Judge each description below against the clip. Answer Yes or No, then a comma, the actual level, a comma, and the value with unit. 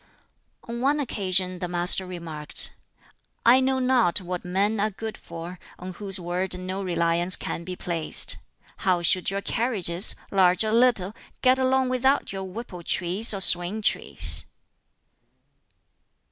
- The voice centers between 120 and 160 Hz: No, high, 190 Hz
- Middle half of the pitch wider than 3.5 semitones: Yes, average, 4.3 semitones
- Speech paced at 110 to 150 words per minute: Yes, average, 140 wpm